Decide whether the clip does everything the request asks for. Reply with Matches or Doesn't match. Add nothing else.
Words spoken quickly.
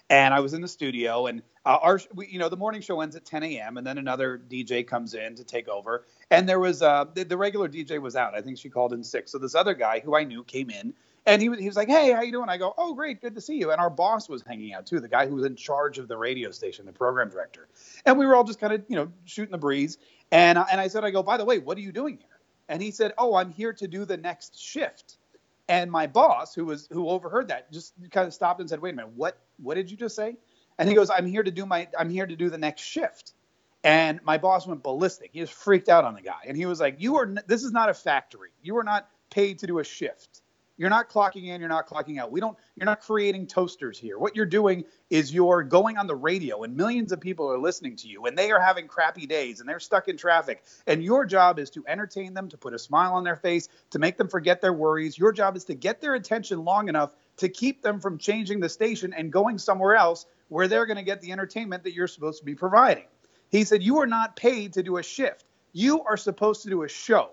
Matches